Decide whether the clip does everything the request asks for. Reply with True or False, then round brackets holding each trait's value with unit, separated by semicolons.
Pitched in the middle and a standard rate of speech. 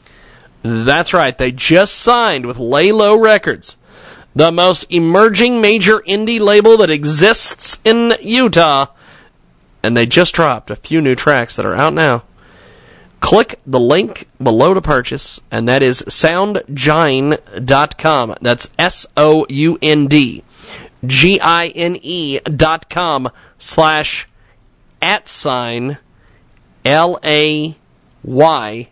False (155 Hz; 100 wpm)